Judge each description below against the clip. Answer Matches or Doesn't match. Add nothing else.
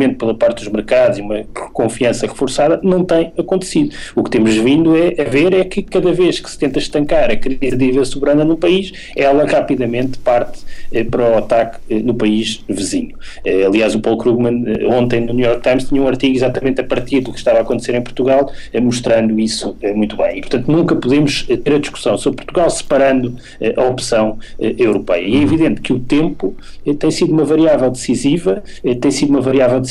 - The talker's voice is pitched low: Matches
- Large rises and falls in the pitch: Doesn't match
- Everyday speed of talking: Doesn't match